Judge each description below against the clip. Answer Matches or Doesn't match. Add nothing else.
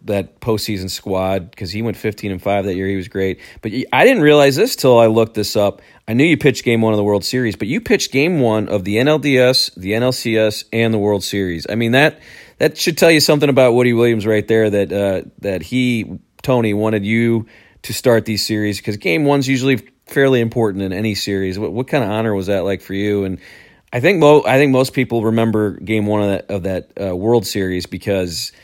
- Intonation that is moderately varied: Matches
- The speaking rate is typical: Doesn't match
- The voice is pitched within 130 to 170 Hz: Doesn't match